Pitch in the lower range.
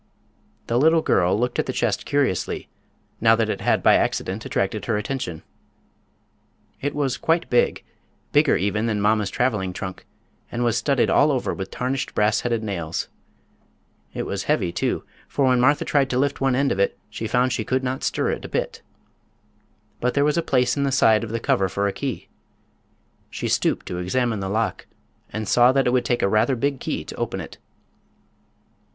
Yes: low, 120 Hz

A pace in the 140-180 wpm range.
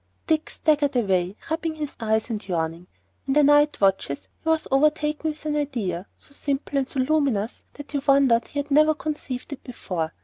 No: average, 190 wpm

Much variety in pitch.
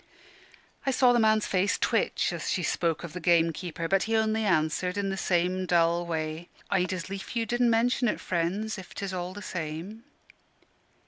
No: average, 4.1 semitones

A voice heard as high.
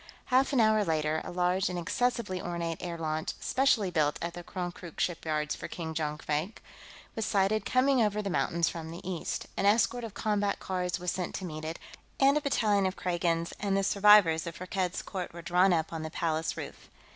No: medium, 180 Hz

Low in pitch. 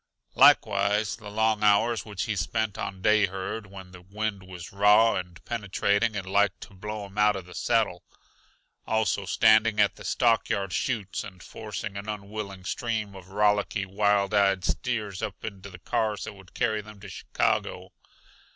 Yes: low, 100 Hz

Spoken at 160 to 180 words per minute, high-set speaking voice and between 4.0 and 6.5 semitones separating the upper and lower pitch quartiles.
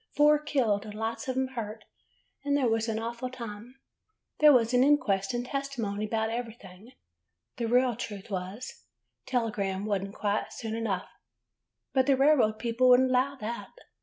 No: average, 175 wpm; high, 230 Hz; average, 3.3 semitones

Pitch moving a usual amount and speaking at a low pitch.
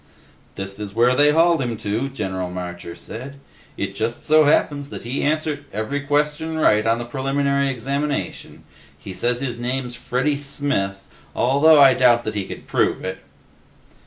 Yes: average, 4.8 semitones; low, 130 Hz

